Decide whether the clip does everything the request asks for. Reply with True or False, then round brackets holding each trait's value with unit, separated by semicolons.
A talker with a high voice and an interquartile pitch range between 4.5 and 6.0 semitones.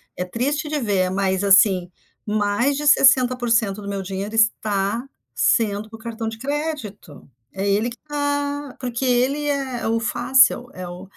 True (230 Hz; 4.9 semitones)